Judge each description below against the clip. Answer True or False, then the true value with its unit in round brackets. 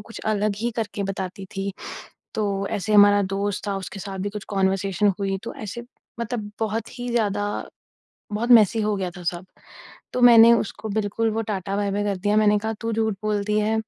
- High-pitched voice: True (205 Hz)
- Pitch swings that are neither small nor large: False (1.8 semitones)